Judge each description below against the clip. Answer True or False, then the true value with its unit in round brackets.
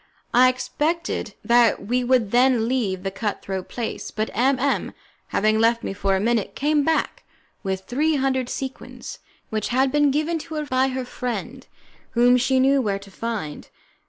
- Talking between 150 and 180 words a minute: True (170 wpm)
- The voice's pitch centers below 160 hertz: False (245 Hz)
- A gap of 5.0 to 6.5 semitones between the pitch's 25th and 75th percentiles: False (3.7 semitones)